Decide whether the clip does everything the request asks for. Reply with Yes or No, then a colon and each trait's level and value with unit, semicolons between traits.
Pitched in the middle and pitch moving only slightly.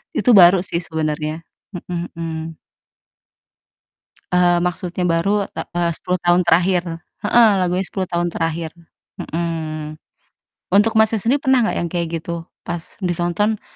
Yes: medium, 175 Hz; narrow, 2.2 semitones